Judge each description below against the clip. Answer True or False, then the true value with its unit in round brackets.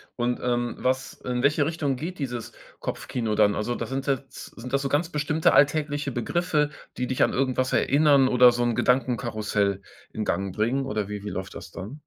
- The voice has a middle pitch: False (125 Hz)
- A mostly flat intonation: False (3.6 semitones)